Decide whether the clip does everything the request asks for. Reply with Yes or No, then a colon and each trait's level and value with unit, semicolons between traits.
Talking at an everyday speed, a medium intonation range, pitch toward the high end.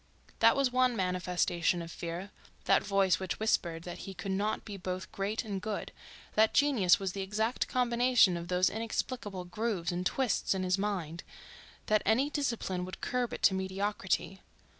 Yes: average, 170 wpm; average, 3.5 semitones; high, 195 Hz